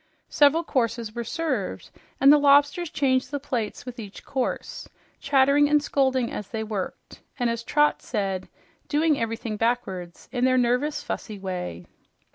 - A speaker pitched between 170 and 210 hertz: No, very high, 250 Hz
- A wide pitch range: No, average, 4.6 semitones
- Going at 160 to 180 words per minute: No, average, 150 wpm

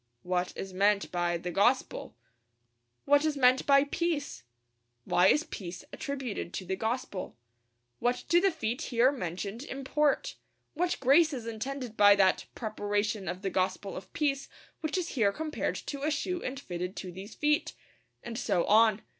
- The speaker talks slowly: No, average, 165 wpm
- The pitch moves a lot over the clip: Yes, wide, 6.6 semitones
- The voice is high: Yes, high, 230 Hz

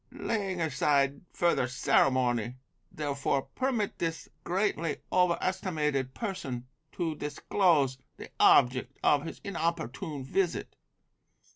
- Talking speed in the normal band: No, slow, 100 wpm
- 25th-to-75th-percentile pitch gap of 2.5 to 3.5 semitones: No, average, 5.2 semitones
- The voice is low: No, medium, 150 Hz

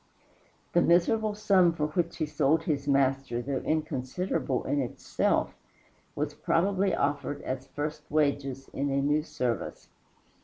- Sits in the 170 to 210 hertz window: No, medium, 145 Hz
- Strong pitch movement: No, average, 3.6 semitones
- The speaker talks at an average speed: No, slow, 130 wpm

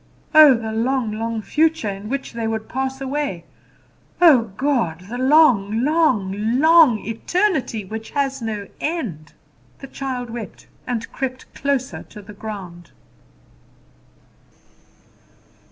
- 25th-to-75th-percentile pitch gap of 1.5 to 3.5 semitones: No, average, 4.3 semitones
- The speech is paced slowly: Yes, slow, 120 wpm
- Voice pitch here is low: No, high, 240 Hz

